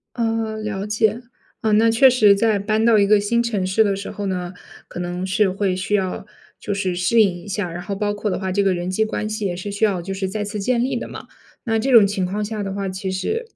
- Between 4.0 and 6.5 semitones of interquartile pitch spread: No, narrow, 2.4 semitones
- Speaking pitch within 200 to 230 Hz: Yes, high, 205 Hz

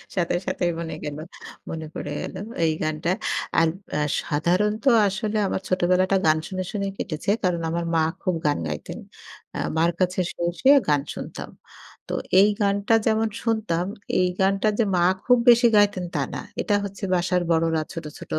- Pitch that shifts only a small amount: No, average, 3.4 semitones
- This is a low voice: No, medium, 180 Hz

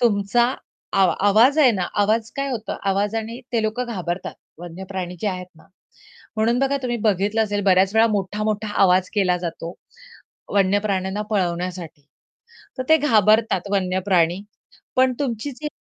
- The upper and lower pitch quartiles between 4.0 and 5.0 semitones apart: No, average, 3.5 semitones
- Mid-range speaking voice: No, high, 205 Hz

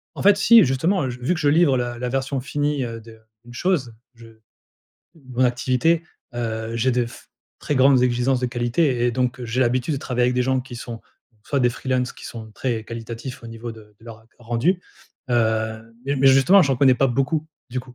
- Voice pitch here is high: No, low, 125 Hz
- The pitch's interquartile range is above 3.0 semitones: No, narrow, 2.4 semitones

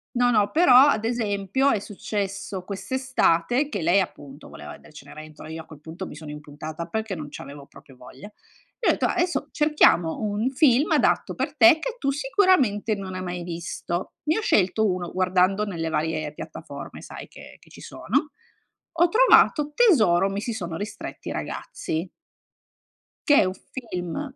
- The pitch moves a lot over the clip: Yes, wide, 7.7 semitones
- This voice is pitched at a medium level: No, high, 195 Hz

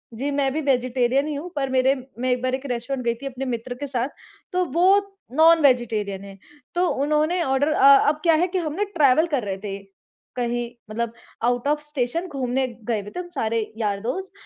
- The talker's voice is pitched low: No, very high, 265 Hz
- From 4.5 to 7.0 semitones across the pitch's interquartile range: No, average, 4.1 semitones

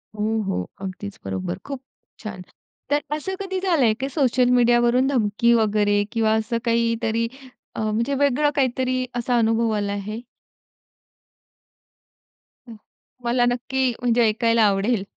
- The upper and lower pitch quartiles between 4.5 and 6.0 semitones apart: No, average, 3.0 semitones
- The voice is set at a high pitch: Yes, high, 235 Hz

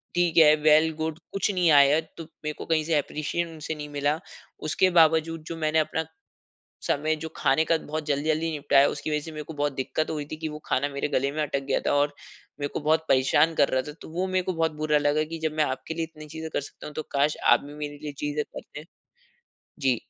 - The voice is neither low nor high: Yes, medium, 155 Hz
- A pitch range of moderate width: No, narrow, 1.7 semitones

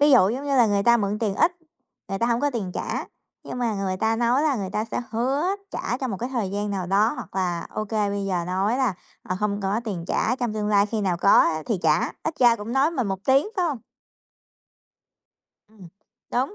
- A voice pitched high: Yes, high, 215 Hz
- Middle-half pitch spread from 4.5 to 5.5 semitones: No, average, 3.9 semitones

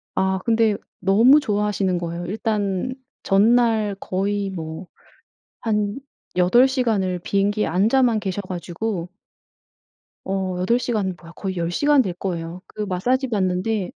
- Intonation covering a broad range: No, average, 3.4 semitones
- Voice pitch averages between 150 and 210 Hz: Yes, high, 200 Hz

